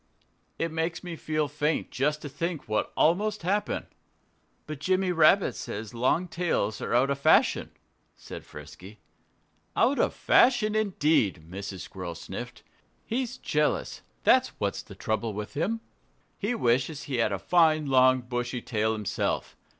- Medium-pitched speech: Yes, medium, 150 Hz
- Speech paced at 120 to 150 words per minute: Yes, average, 145 wpm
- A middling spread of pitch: No, wide, 7.6 semitones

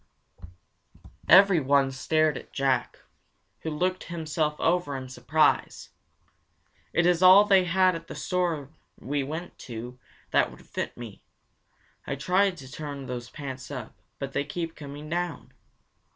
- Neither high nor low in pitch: Yes, medium, 150 Hz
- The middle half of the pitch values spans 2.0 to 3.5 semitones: No, average, 4.5 semitones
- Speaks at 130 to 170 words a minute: Yes, slow, 135 wpm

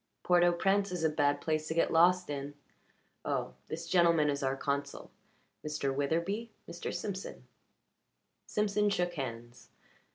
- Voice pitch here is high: No, medium, 165 Hz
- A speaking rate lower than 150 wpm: Yes, average, 140 wpm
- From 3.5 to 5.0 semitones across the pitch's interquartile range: Yes, average, 4.0 semitones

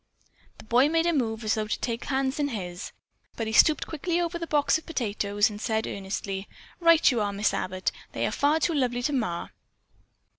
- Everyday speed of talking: No, fast, 215 wpm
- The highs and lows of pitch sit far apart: Yes, wide, 6.3 semitones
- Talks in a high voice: Yes, high, 240 Hz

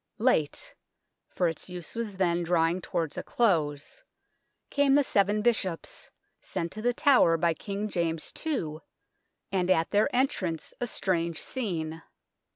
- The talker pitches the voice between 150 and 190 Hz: Yes, medium, 185 Hz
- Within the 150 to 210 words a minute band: No, average, 140 wpm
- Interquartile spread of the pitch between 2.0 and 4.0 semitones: No, wide, 5.5 semitones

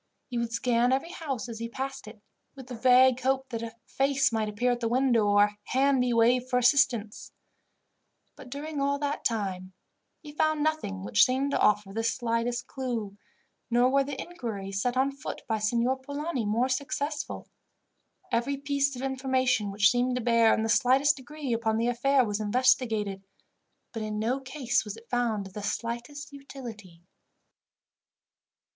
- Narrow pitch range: No, average, 3.3 semitones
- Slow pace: No, average, 175 wpm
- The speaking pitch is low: No, high, 245 Hz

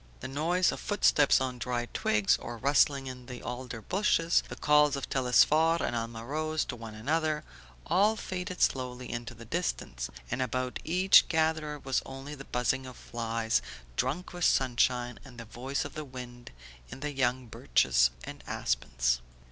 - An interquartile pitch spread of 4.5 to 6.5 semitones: No, average, 3.9 semitones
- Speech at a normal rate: Yes, average, 165 wpm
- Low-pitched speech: Yes, low, 130 Hz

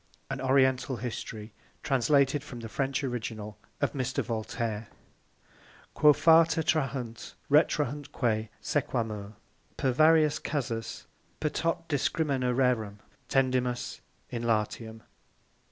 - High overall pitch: No, low, 130 Hz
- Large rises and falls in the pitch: No, average, 4.2 semitones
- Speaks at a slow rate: Yes, slow, 100 wpm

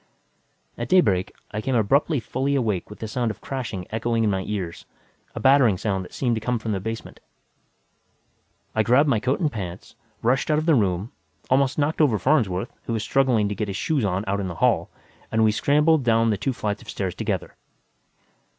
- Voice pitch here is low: Yes, low, 115 Hz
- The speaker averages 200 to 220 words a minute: Yes, fast, 205 wpm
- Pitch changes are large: No, average, 4.7 semitones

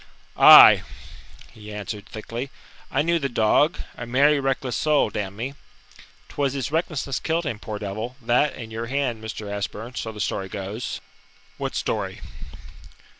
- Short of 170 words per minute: Yes, average, 155 wpm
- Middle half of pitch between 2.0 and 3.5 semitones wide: No, average, 4.6 semitones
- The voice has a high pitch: No, low, 120 Hz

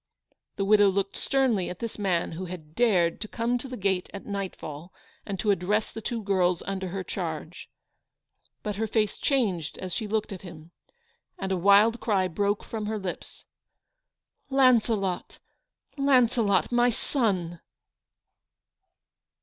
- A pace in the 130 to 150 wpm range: Yes, average, 145 wpm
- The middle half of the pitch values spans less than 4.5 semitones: Yes, average, 3.5 semitones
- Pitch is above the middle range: Yes, high, 200 Hz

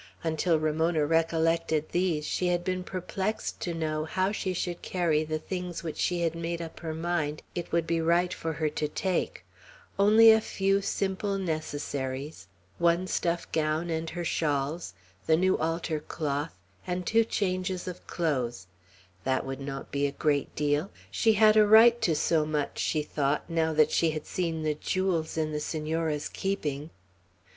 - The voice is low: No, medium, 165 Hz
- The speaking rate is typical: Yes, average, 170 wpm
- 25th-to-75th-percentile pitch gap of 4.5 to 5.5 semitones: No, average, 2.9 semitones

